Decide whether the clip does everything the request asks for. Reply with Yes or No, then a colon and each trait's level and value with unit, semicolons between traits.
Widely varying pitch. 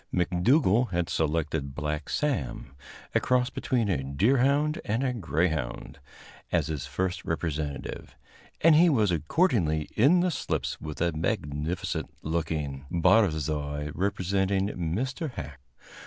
Yes: wide, 7.3 semitones